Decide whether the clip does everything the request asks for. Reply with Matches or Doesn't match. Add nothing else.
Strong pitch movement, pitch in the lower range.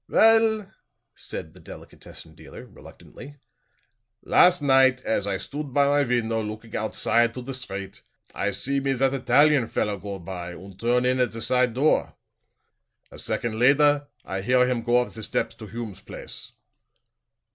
Doesn't match